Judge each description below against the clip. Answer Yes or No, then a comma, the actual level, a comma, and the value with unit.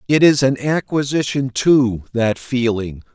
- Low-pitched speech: Yes, low, 130 Hz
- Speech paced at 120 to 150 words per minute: Yes, slow, 135 wpm